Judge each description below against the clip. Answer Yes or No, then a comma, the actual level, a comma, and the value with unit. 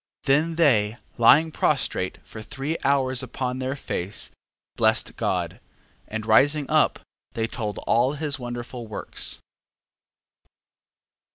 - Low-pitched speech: Yes, low, 130 Hz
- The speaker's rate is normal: No, slow, 115 wpm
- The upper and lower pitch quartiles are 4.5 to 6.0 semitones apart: No, average, 4.0 semitones